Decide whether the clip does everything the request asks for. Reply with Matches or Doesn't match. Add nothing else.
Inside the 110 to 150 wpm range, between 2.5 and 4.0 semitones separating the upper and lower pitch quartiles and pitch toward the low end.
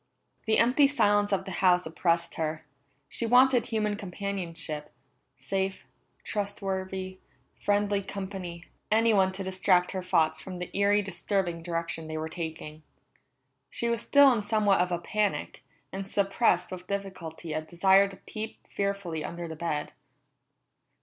Doesn't match